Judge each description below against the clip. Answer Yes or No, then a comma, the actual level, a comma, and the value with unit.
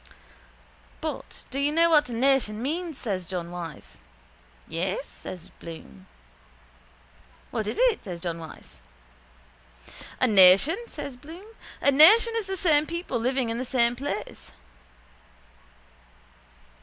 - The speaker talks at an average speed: No, slow, 125 wpm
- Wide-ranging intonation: Yes, wide, 8.9 semitones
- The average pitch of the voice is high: Yes, very high, 250 Hz